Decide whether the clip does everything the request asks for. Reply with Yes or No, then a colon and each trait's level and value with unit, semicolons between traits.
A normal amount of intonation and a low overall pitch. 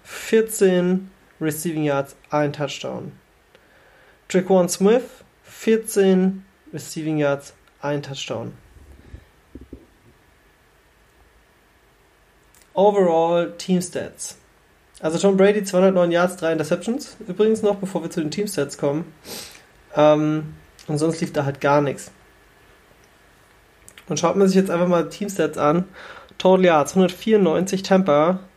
No: average, 3.9 semitones; medium, 175 Hz